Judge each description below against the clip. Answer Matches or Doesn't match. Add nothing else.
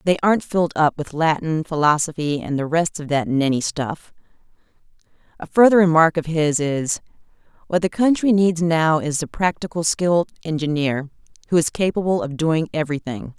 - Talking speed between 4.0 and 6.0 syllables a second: Matches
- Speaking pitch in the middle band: Matches